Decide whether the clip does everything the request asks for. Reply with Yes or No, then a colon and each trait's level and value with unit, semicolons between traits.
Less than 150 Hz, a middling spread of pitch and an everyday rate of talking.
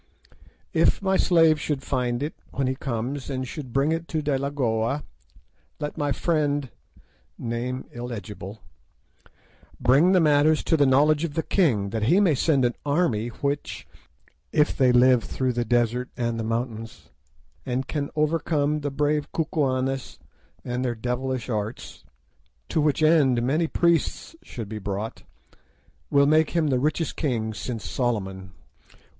Yes: low, 135 Hz; average, 4.0 semitones; average, 145 wpm